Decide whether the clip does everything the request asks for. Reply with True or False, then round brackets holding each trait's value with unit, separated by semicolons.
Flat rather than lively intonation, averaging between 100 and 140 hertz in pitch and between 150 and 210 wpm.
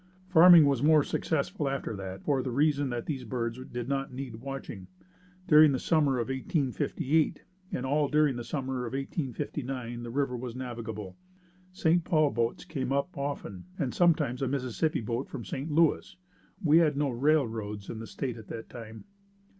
False (4.0 semitones; 135 Hz; 170 wpm)